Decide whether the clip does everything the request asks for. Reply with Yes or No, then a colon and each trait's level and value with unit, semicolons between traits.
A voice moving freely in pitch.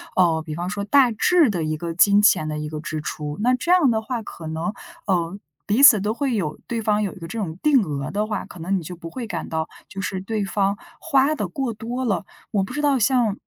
Yes: wide, 6.1 semitones